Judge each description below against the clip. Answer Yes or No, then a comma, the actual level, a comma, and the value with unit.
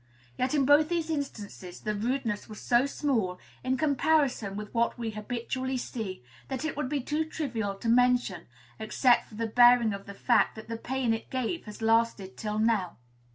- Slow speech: No, average, 185 wpm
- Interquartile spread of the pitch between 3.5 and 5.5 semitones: Yes, average, 3.8 semitones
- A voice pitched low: No, high, 235 Hz